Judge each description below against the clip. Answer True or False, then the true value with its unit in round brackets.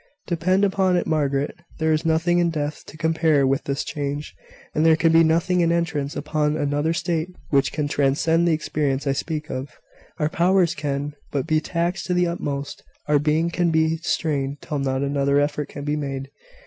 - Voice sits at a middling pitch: True (155 Hz)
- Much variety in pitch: False (2.7 semitones)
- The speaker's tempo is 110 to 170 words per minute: False (195 wpm)